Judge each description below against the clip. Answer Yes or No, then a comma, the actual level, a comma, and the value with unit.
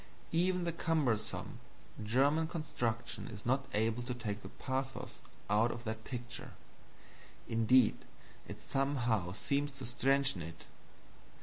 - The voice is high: No, low, 120 Hz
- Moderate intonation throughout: Yes, average, 3.9 semitones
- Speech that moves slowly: Yes, slow, 120 wpm